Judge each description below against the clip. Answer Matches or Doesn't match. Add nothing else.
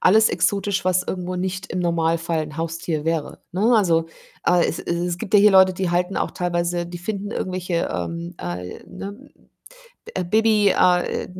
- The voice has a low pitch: Doesn't match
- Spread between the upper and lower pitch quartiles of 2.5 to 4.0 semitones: Doesn't match